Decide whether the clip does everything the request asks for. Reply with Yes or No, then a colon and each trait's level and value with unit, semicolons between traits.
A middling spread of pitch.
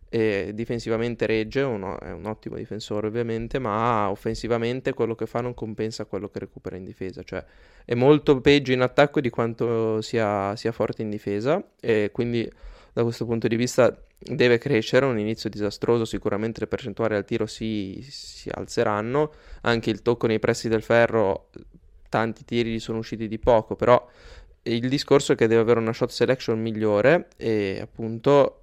No: narrow, 1.8 semitones